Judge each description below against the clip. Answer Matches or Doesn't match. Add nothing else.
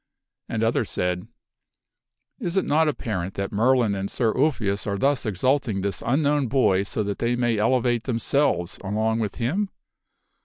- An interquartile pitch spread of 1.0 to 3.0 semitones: Doesn't match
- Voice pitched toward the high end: Doesn't match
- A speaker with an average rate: Matches